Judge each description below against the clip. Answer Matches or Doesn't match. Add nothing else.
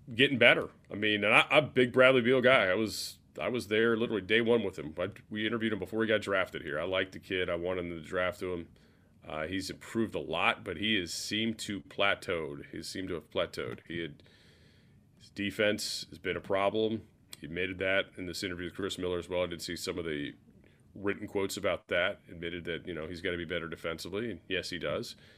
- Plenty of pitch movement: Doesn't match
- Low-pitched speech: Matches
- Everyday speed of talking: Doesn't match